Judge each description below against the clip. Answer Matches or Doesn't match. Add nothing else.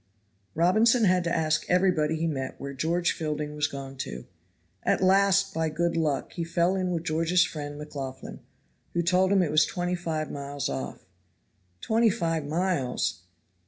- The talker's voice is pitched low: Doesn't match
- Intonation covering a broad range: Doesn't match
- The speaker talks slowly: Doesn't match